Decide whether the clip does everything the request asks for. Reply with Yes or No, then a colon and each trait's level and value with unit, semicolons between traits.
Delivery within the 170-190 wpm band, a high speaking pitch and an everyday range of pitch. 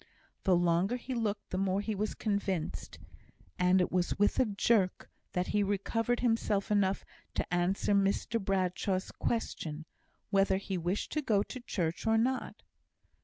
No: average, 155 wpm; high, 200 Hz; average, 3.2 semitones